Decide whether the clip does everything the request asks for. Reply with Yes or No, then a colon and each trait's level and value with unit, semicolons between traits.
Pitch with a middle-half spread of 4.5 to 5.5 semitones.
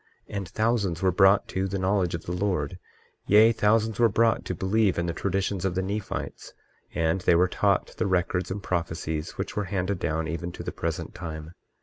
No: average, 2.9 semitones